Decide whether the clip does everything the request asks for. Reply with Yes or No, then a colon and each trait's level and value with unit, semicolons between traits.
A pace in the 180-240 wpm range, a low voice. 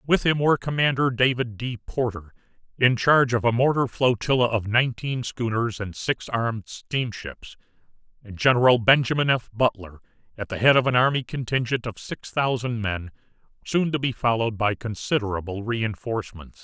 No: average, 155 wpm; low, 120 Hz